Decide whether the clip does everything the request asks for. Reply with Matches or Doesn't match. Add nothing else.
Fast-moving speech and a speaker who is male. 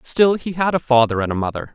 Matches